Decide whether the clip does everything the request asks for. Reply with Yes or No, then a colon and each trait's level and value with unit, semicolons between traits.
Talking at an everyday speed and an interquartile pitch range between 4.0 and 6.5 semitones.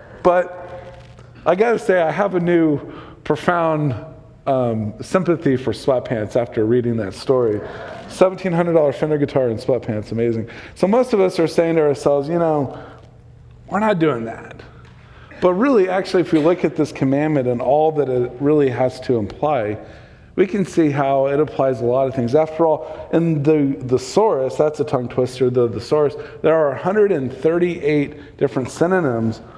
Yes: average, 160 wpm; average, 4.7 semitones